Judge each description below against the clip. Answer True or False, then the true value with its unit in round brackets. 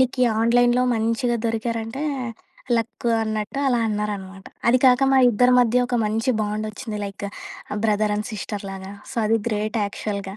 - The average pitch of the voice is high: True (220 Hz)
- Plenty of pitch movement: False (2.5 semitones)